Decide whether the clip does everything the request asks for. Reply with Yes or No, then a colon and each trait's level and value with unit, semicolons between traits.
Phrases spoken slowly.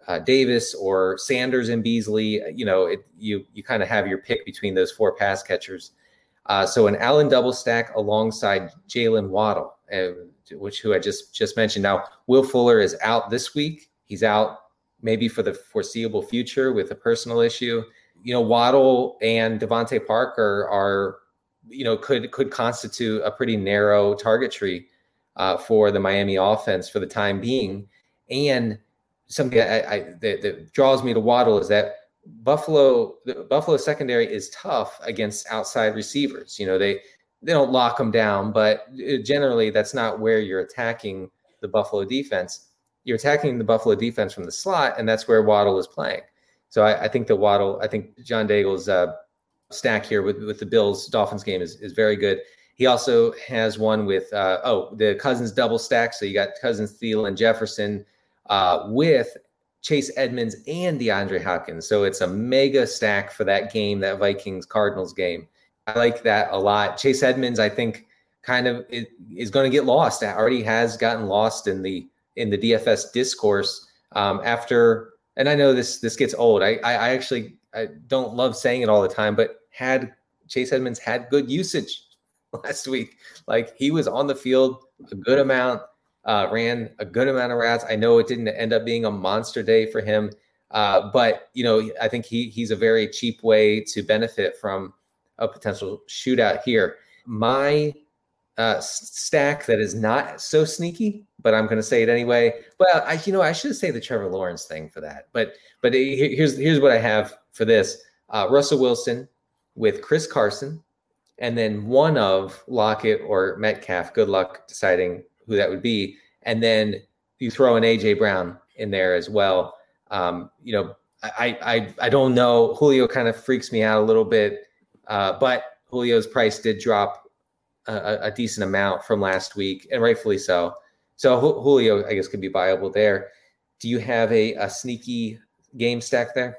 No: average, 180 wpm